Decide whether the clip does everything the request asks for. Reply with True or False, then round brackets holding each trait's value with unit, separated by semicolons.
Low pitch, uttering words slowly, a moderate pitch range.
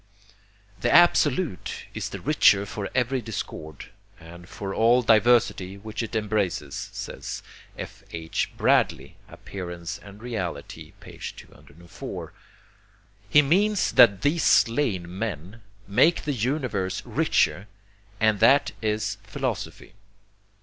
True (110 Hz; 110 wpm; 4.8 semitones)